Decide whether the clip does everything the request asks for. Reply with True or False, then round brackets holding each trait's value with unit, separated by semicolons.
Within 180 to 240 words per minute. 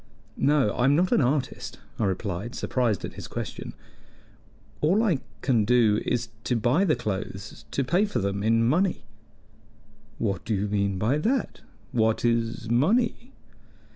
False (155 wpm)